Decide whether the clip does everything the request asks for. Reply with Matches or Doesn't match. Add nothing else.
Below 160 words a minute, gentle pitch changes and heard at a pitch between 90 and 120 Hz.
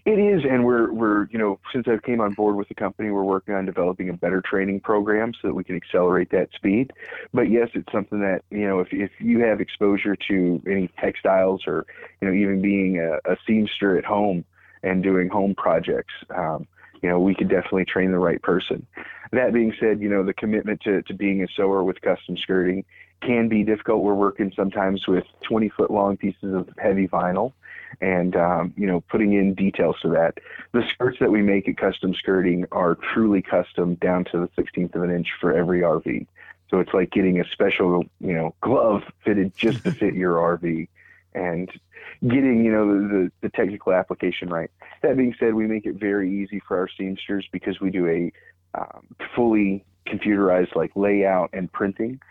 Doesn't match